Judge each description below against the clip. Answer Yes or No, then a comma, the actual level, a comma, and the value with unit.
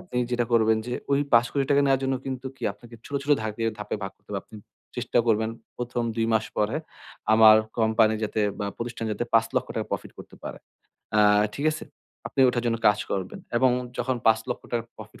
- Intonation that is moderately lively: No, narrow, 2.2 semitones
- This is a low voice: Yes, low, 115 Hz